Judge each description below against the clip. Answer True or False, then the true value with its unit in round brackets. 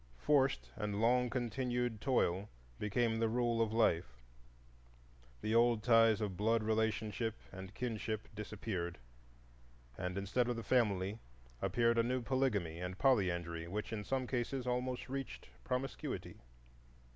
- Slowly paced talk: True (130 wpm)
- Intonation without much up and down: False (3.2 semitones)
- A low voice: True (115 Hz)